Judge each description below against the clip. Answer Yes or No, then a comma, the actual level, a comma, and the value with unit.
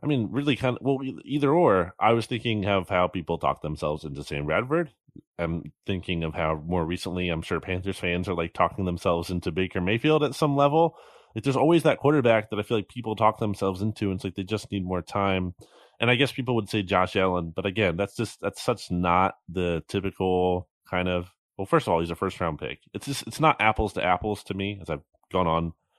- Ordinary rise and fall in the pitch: Yes, average, 4.5 semitones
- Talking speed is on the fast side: Yes, fast, 235 wpm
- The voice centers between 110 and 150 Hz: No, very low, 95 Hz